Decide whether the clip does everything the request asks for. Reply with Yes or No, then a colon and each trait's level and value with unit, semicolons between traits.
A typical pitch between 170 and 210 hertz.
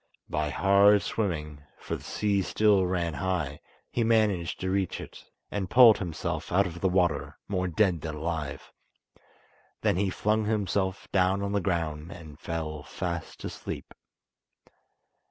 No: very low, 90 Hz